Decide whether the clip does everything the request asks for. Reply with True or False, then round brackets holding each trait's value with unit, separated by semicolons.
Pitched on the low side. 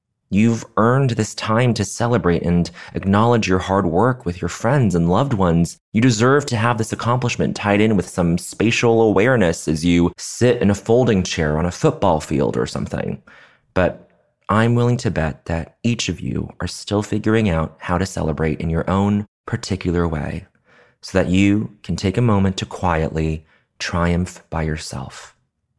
True (95 Hz)